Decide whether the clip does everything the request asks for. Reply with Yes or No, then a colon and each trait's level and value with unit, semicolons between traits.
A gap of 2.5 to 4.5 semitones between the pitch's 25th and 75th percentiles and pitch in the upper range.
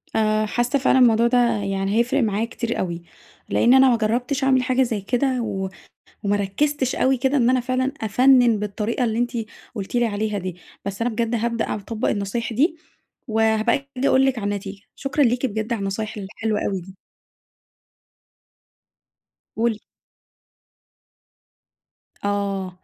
Yes: average, 3.7 semitones; high, 225 Hz